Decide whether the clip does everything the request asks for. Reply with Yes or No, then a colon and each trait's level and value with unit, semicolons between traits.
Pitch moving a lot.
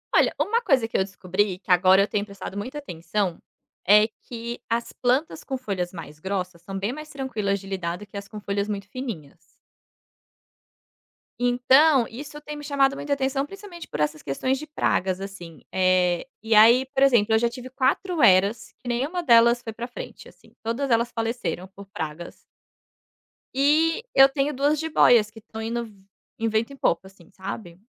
Yes: wide, 5.7 semitones